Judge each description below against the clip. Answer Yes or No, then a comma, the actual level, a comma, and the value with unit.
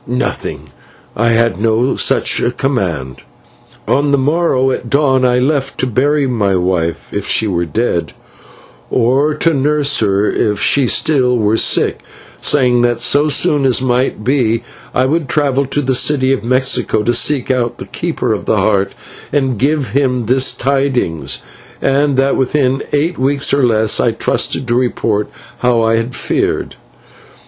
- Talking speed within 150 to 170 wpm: Yes, average, 160 wpm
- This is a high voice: No, low, 130 Hz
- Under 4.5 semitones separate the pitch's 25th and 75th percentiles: Yes, average, 3.4 semitones